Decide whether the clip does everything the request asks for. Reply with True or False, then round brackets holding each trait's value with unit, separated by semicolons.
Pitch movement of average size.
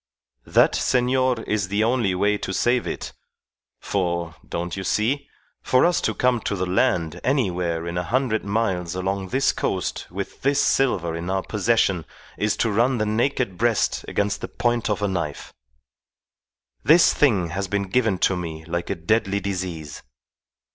True (4.9 semitones)